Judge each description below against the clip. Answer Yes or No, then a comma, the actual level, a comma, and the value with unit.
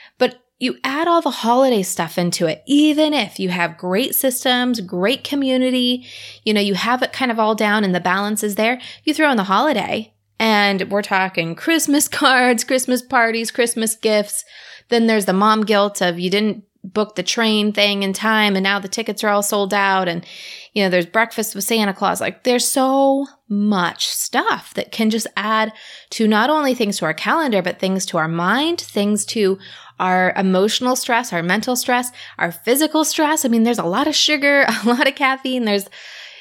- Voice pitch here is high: Yes, high, 220 Hz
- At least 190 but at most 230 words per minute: Yes, average, 195 wpm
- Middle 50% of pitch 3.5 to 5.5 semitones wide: Yes, average, 4.5 semitones